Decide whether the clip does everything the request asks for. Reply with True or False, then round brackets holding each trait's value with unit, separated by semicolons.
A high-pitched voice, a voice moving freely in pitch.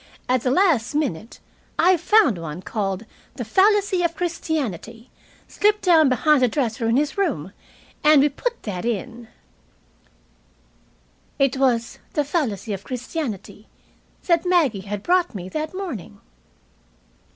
True (265 Hz; 7.3 semitones)